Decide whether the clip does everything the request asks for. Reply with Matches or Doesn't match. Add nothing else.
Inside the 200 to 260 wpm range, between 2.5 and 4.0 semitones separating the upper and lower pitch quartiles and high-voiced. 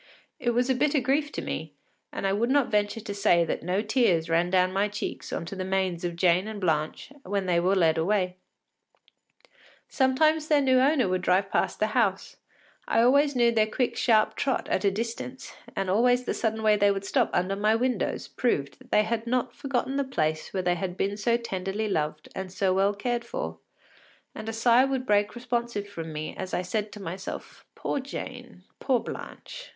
Doesn't match